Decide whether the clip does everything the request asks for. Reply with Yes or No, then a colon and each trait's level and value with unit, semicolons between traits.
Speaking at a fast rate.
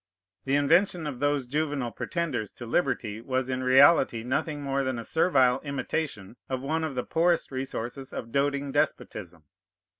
No: average, 155 wpm